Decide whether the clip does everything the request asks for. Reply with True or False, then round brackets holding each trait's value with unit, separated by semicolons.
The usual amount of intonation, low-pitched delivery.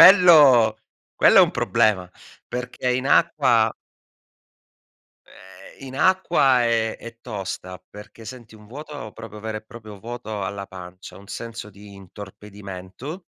True (3.9 semitones; 110 Hz)